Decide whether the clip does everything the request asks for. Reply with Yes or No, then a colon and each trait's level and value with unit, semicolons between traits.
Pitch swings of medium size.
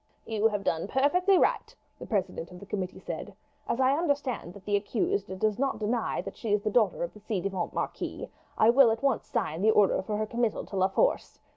Yes: average, 4.5 semitones